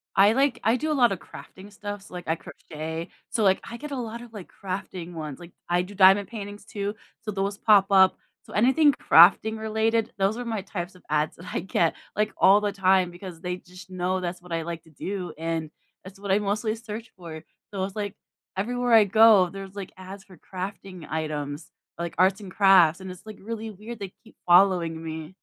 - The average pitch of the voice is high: Yes, high, 195 Hz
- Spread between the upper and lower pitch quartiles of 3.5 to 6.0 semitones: No, average, 3.1 semitones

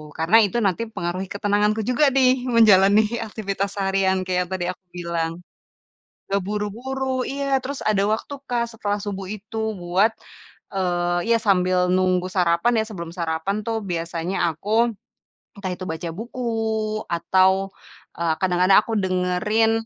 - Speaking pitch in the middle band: No, high, 195 Hz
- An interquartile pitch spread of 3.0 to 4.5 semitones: Yes, average, 3.5 semitones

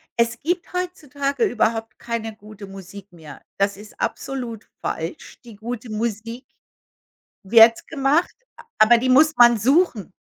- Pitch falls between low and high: No, high, 230 Hz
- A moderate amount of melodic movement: Yes, average, 3.6 semitones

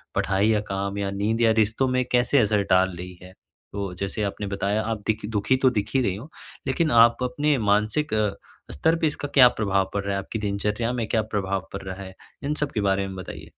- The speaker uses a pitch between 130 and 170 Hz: No, low, 105 Hz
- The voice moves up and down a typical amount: Yes, average, 3.4 semitones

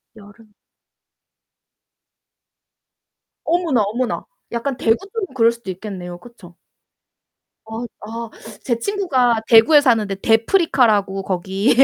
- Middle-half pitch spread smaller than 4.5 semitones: Yes, average, 3.8 semitones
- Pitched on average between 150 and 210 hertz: No, high, 230 Hz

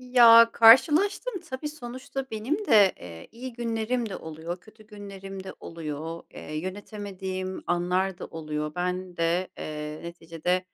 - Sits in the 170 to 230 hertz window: Yes, high, 190 Hz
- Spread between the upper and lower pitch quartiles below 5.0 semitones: No, wide, 5.4 semitones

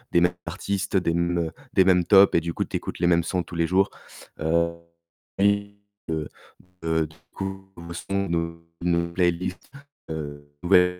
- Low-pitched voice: Yes, very low, 85 Hz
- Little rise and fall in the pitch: Yes, narrow, 2.2 semitones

